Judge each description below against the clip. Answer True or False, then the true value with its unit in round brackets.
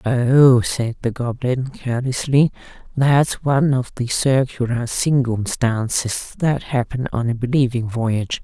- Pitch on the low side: True (125 Hz)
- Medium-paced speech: False (120 wpm)